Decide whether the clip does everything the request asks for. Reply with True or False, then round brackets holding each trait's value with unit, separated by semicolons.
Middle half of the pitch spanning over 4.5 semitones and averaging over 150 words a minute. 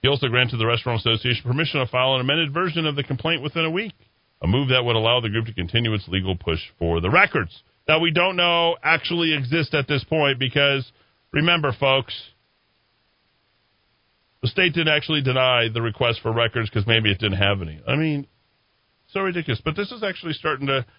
True (5.3 semitones; 200 wpm)